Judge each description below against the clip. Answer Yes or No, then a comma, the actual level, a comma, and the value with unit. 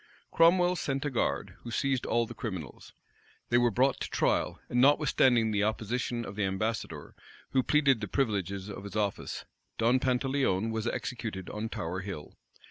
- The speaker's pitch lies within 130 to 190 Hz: No, low, 115 Hz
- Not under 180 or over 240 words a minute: No, average, 165 wpm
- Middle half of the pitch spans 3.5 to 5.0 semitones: Yes, average, 4.3 semitones